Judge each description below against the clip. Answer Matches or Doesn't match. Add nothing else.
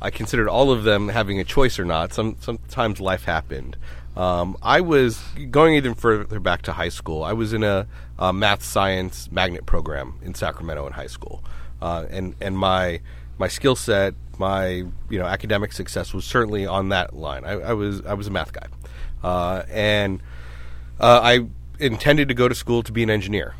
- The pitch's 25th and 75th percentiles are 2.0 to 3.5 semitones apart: Doesn't match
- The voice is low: Matches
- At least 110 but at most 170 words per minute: Doesn't match